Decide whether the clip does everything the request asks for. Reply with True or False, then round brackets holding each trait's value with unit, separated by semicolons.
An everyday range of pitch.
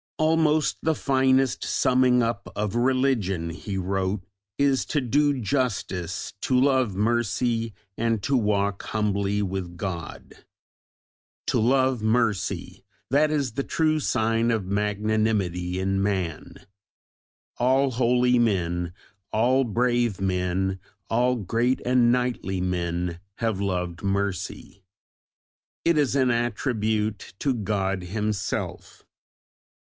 True (4.7 semitones)